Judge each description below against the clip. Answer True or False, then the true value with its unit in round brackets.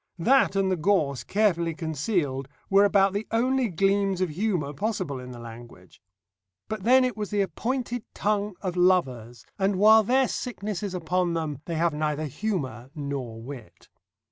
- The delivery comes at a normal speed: True (165 wpm)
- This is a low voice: False (185 Hz)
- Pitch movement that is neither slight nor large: False (6.2 semitones)